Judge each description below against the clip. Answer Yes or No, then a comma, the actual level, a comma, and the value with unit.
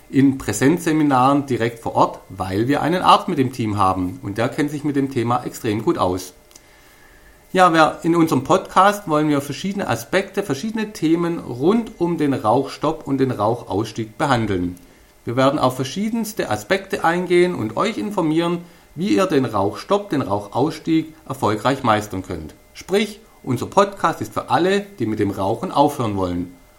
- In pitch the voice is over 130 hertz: Yes, medium, 140 Hz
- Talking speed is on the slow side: No, average, 160 wpm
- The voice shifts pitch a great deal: Yes, wide, 8.0 semitones